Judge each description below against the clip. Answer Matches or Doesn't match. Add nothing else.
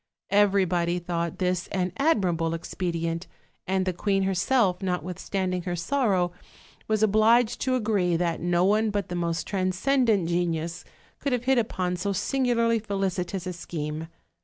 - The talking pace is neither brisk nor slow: Matches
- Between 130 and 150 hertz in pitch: Doesn't match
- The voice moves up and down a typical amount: Matches